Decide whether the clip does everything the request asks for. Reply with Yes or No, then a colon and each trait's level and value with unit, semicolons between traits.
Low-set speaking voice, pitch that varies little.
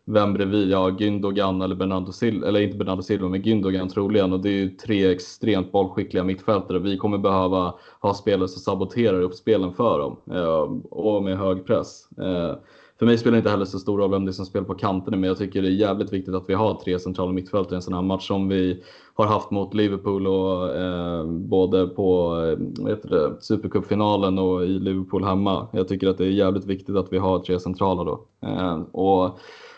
Yes: very low, 95 Hz; narrow, 1.4 semitones